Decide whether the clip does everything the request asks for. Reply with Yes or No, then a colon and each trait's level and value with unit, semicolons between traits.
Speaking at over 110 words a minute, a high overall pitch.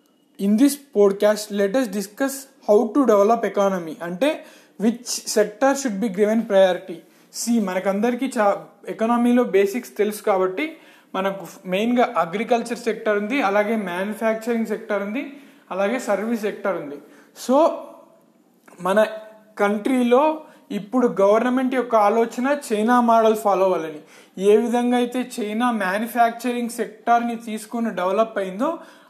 Yes: average, 120 wpm; high, 225 Hz